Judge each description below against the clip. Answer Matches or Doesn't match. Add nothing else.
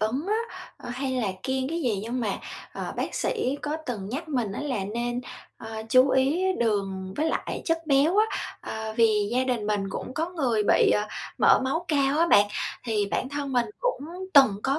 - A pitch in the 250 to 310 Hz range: Matches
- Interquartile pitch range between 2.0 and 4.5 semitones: Doesn't match